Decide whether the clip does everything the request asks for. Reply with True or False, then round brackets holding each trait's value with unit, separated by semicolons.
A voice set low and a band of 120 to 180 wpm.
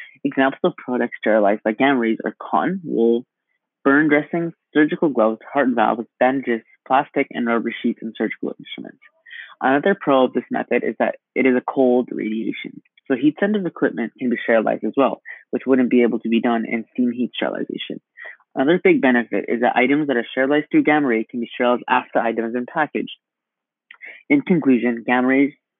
False (125 Hz; 190 wpm)